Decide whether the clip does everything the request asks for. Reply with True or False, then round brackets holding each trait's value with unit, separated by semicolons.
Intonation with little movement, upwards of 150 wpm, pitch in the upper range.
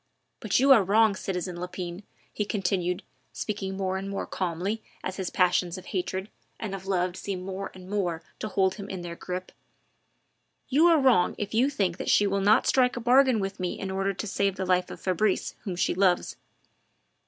True (2.3 semitones; 200 wpm; 195 Hz)